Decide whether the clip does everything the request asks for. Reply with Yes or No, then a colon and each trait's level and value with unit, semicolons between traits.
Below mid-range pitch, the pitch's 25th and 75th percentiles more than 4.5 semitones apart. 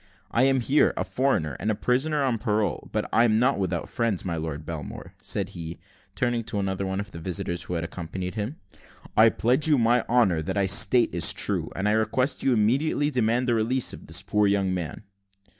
Yes: low, 110 Hz; average, 4.9 semitones